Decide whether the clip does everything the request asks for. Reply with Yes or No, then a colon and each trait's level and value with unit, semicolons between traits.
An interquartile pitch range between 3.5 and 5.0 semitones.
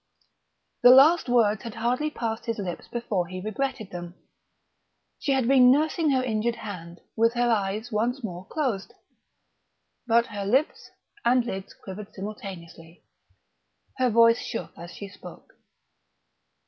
Yes: average, 4.2 semitones